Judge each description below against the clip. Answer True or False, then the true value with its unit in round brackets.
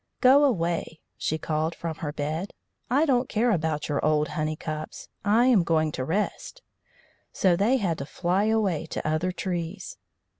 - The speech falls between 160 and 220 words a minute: True (165 wpm)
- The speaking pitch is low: False (170 Hz)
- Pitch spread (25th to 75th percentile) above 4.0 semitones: True (5.4 semitones)